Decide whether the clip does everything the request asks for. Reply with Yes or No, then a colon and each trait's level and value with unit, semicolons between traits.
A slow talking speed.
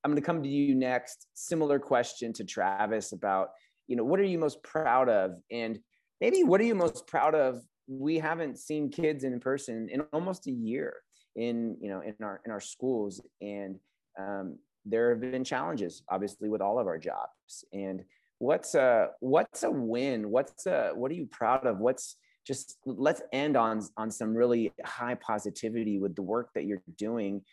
No: average, 190 wpm